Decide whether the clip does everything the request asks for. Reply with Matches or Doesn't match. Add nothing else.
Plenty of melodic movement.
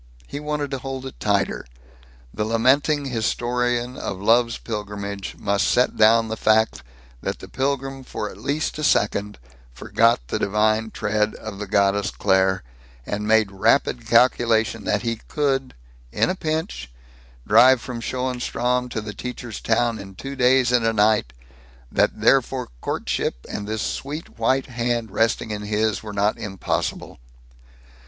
Doesn't match